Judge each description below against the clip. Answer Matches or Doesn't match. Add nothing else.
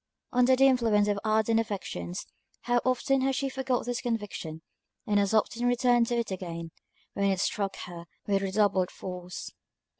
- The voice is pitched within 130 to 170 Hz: Doesn't match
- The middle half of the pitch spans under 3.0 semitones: Doesn't match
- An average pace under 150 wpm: Doesn't match